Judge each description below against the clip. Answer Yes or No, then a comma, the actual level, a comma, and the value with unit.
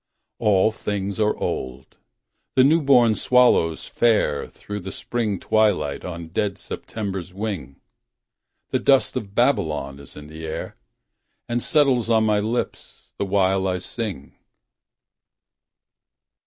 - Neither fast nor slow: No, slow, 125 wpm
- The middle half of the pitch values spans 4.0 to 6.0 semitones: Yes, average, 4.3 semitones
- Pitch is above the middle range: No, low, 100 Hz